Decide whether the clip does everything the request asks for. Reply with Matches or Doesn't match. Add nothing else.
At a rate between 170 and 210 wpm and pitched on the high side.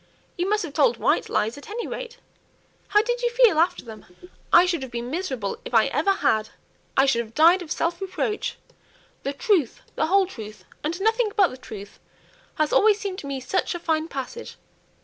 Matches